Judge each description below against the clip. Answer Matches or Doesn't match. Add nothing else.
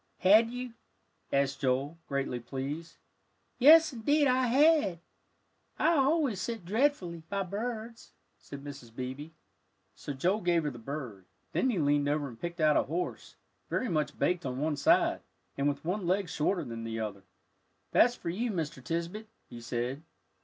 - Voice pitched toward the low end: Doesn't match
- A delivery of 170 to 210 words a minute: Doesn't match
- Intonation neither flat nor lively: Doesn't match